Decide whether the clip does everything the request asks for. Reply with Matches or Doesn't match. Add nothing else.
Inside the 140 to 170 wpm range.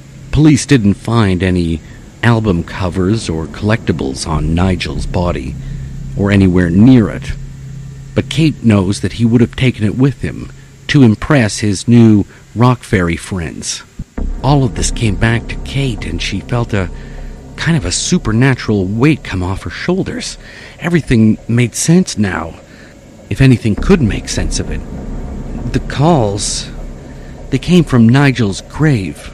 Matches